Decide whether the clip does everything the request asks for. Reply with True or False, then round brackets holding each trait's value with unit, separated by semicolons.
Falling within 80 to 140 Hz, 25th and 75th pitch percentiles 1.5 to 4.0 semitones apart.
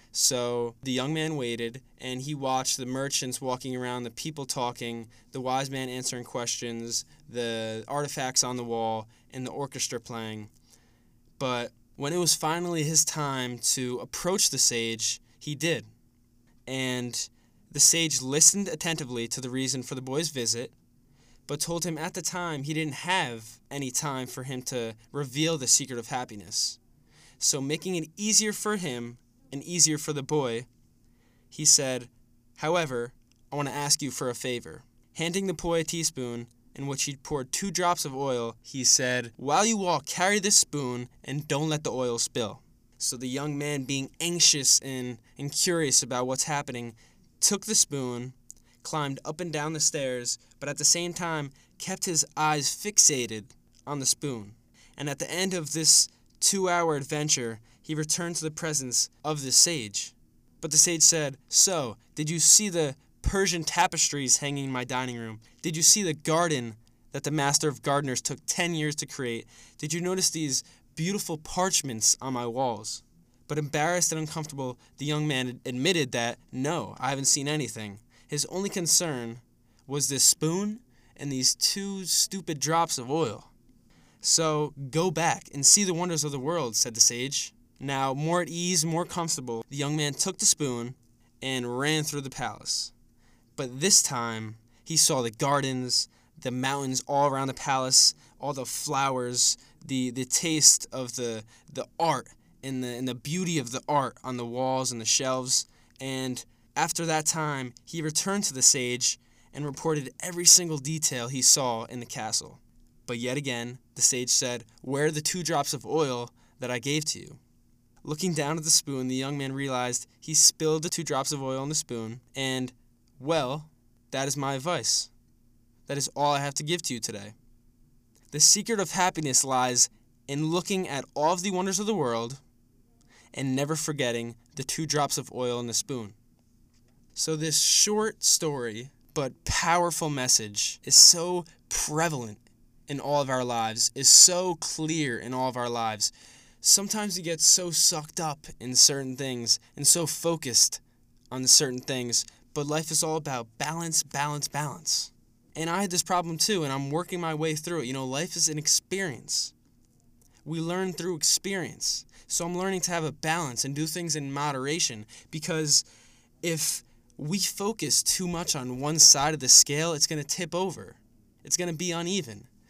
False (135 Hz; 4.6 semitones)